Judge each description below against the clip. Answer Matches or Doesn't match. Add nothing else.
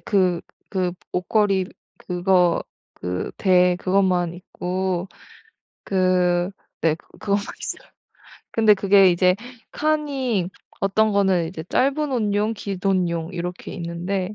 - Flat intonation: Matches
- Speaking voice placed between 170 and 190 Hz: Matches